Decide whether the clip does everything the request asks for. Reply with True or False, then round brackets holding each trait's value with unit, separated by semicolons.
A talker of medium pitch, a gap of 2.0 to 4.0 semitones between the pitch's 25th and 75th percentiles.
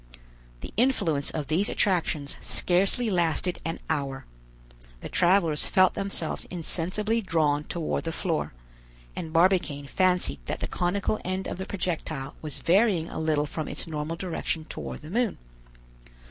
True (170 Hz; 3.4 semitones)